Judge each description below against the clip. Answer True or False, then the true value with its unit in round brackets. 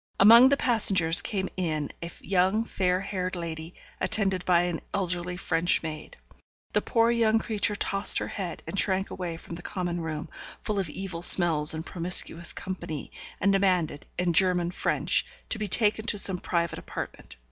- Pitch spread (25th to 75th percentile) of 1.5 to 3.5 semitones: True (2.6 semitones)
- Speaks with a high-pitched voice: False (180 Hz)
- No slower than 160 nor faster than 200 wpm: True (170 wpm)